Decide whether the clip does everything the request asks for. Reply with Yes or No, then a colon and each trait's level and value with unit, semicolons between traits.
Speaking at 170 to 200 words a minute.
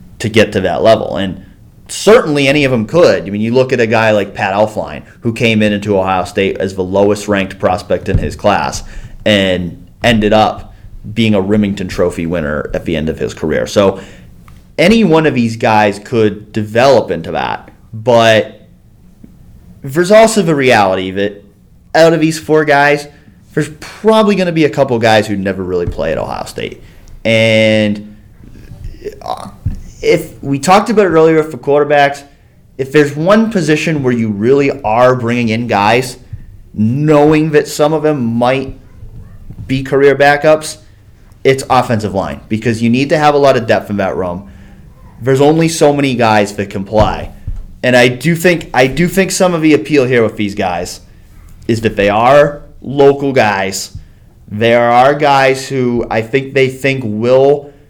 Yes: average, 175 wpm